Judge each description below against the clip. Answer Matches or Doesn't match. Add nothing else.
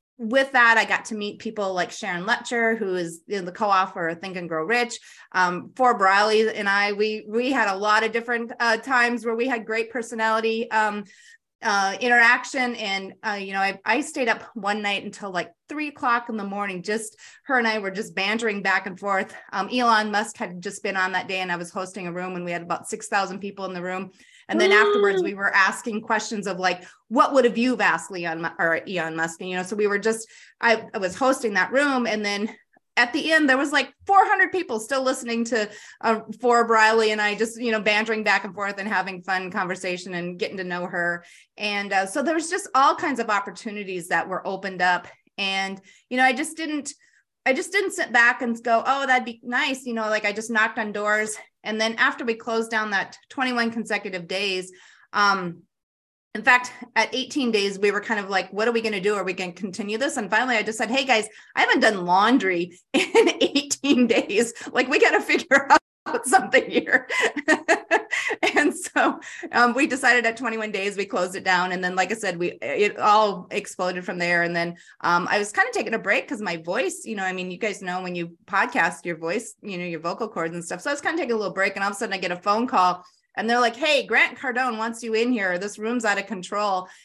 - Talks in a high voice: Matches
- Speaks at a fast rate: Matches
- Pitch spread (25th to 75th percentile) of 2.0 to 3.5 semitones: Doesn't match